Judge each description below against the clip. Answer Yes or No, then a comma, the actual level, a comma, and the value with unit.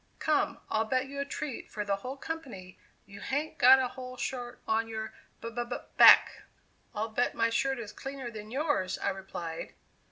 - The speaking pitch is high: Yes, high, 240 Hz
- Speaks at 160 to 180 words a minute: No, average, 190 wpm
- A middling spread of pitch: Yes, average, 3.9 semitones